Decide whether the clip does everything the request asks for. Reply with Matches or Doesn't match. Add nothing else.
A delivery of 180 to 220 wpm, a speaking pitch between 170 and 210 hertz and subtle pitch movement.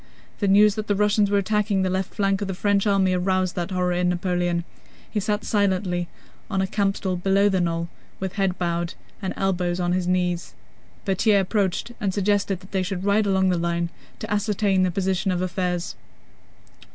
Matches